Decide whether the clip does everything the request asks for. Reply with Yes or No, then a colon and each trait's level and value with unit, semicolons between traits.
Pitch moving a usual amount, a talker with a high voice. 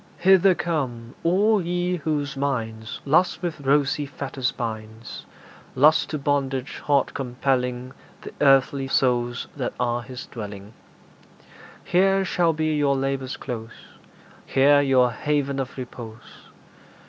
No: average, 3.4 semitones; low, 135 Hz